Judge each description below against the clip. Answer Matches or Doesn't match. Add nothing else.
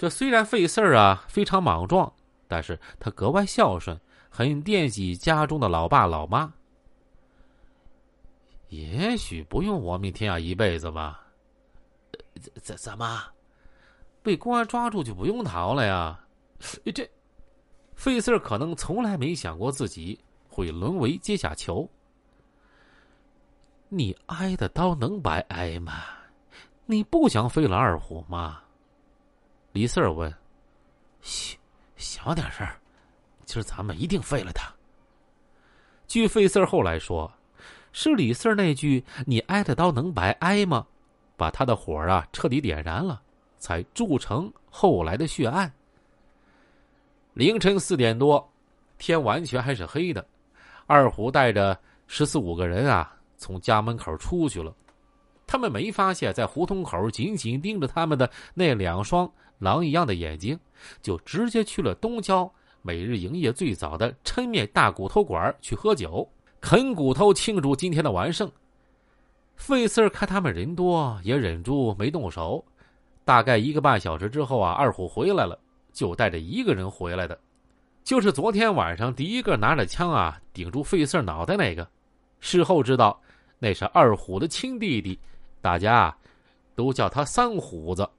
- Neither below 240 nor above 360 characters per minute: Doesn't match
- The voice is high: Doesn't match